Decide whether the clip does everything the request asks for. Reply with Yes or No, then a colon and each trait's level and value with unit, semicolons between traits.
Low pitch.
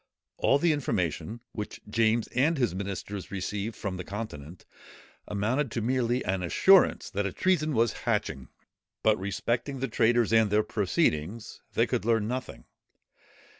Yes: low, 110 Hz